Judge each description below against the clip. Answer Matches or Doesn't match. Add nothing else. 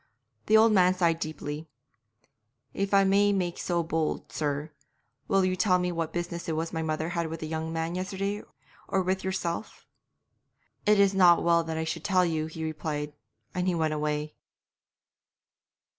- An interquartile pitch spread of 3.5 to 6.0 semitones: Doesn't match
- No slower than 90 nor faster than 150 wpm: Doesn't match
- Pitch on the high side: Doesn't match